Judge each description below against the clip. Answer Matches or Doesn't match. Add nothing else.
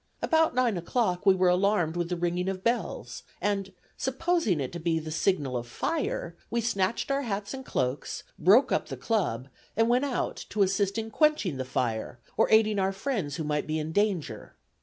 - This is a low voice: Doesn't match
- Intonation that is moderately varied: Doesn't match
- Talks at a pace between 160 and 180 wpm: Doesn't match